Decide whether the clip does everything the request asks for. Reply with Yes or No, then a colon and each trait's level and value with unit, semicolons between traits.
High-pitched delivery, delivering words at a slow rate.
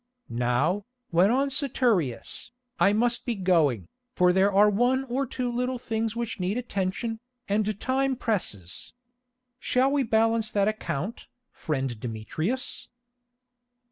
Yes: high, 215 Hz; slow, 125 wpm